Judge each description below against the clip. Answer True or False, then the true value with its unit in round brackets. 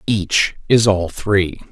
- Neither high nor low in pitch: False (100 Hz)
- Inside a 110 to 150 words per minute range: True (140 wpm)